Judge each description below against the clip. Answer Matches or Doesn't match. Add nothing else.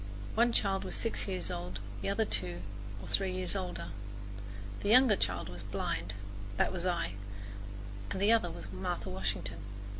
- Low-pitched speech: Doesn't match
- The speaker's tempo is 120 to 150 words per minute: Doesn't match